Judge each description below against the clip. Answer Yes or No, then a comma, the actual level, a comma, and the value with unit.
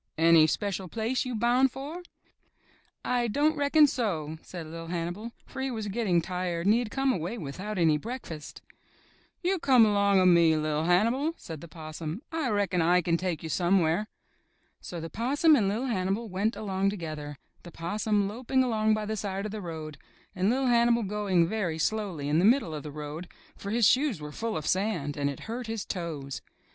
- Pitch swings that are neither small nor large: No, wide, 5.8 semitones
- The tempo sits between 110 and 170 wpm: No, average, 195 wpm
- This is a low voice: No, high, 195 Hz